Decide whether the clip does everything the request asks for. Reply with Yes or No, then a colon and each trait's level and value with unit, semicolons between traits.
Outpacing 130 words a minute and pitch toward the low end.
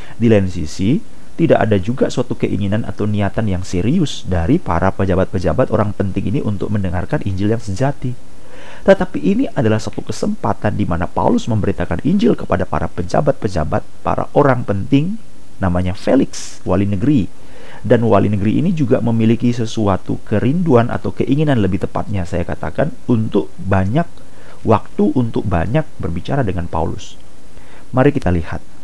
Yes: fast, 140 wpm; low, 105 Hz